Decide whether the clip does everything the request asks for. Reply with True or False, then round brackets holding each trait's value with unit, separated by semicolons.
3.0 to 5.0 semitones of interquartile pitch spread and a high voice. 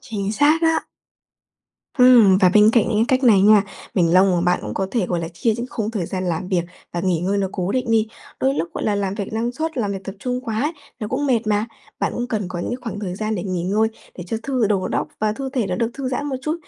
True (4.5 semitones; 210 Hz)